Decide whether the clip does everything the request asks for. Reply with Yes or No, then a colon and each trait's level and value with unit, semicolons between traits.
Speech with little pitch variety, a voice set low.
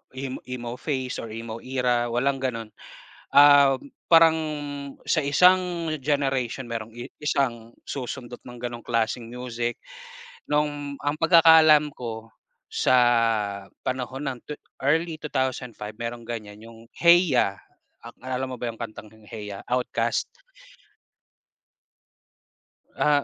No: average, 3.6 semitones; low, 125 Hz